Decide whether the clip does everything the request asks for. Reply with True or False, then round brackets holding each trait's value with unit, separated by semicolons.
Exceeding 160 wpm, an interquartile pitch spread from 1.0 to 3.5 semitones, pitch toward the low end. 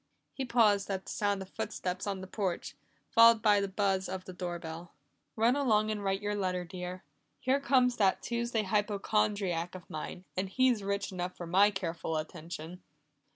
False (175 wpm; 2.9 semitones; 195 Hz)